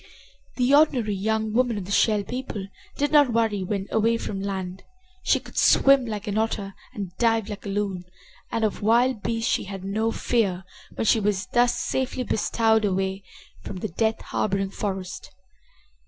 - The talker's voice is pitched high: Yes, high, 215 Hz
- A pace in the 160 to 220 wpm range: Yes, average, 170 wpm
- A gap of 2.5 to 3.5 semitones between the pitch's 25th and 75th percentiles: Yes, average, 2.8 semitones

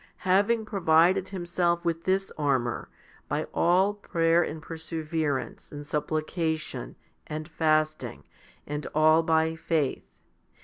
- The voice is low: No, medium, 160 Hz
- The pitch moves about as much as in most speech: No, narrow, 2.1 semitones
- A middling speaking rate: No, slow, 105 wpm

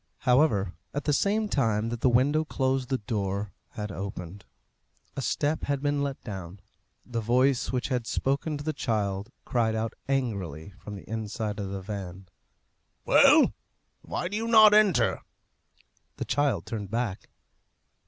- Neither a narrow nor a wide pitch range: No, wide, 5.8 semitones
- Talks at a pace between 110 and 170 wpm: Yes, average, 155 wpm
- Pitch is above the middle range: No, low, 115 Hz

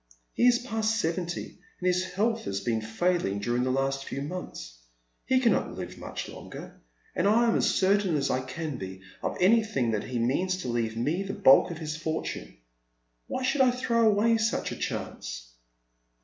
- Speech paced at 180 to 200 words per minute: Yes, average, 185 wpm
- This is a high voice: No, medium, 170 Hz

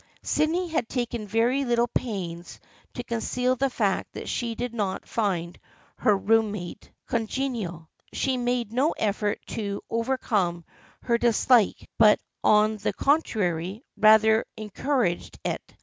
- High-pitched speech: Yes, high, 225 Hz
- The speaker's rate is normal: No, slow, 130 wpm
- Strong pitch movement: No, average, 3.4 semitones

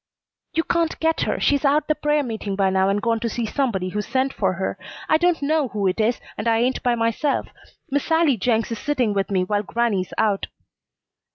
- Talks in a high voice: Yes, high, 235 Hz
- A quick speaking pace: Yes, fast, 215 wpm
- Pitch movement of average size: No, wide, 5.9 semitones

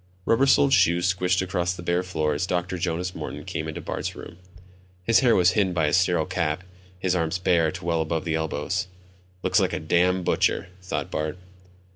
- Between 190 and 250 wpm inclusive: Yes, average, 195 wpm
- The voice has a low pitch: Yes, very low, 90 Hz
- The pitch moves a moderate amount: No, narrow, 2.1 semitones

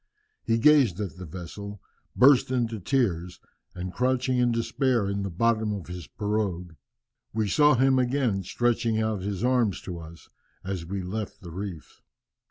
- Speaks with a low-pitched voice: Yes, low, 105 Hz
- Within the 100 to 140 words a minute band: No, average, 160 wpm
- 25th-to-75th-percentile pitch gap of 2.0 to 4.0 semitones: No, average, 4.8 semitones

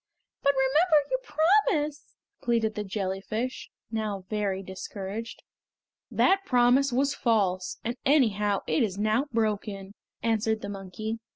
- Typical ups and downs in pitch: Yes, average, 5.0 semitones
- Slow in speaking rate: Yes, slow, 120 wpm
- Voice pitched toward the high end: Yes, high, 220 Hz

